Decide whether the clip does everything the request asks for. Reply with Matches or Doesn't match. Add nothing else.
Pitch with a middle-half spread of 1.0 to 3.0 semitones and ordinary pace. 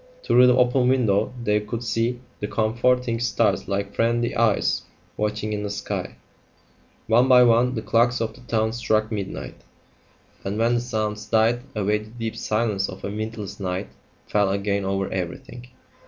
Matches